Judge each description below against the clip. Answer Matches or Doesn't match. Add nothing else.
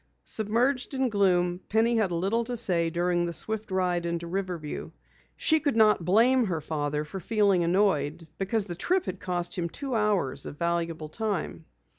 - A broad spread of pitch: Doesn't match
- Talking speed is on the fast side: Doesn't match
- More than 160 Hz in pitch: Matches